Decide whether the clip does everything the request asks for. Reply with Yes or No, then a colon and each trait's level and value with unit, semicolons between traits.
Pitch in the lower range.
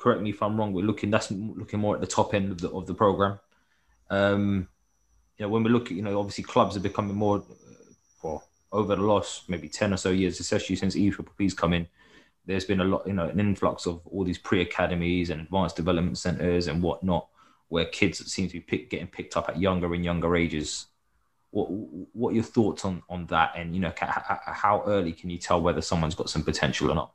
Yes: very low, 95 Hz